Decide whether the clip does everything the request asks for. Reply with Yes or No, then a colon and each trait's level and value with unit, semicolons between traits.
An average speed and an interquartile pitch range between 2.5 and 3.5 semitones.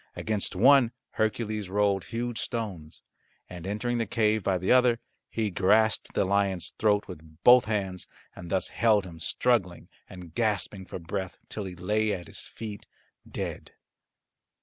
Yes: average, 150 wpm; average, 3.2 semitones